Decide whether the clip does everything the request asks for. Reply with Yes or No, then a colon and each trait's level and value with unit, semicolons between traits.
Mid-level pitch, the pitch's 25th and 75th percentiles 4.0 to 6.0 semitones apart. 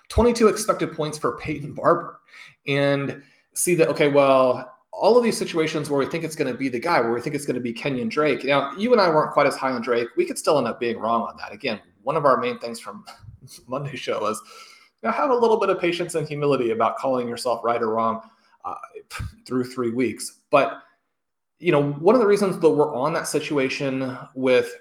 Yes: medium, 145 Hz; wide, 5.5 semitones